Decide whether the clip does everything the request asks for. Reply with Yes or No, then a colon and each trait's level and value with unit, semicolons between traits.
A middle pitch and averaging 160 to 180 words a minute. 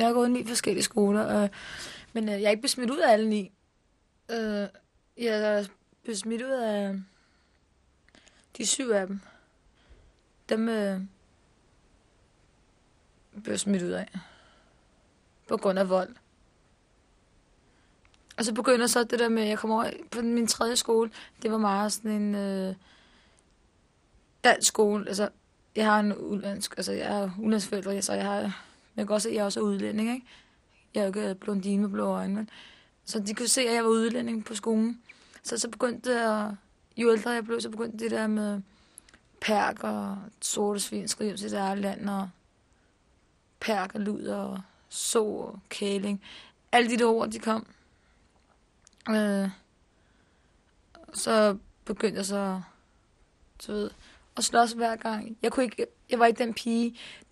No: high, 215 Hz; average, 165 wpm